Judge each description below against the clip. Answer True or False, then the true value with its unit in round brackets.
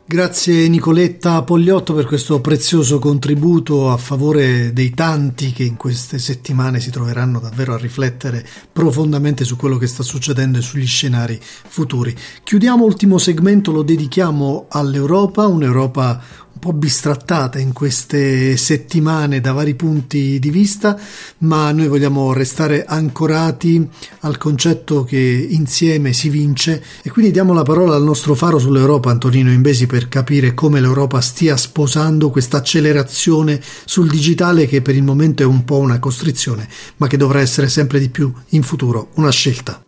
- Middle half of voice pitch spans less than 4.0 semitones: True (3.4 semitones)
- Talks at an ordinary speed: True (150 wpm)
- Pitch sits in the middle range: True (145 Hz)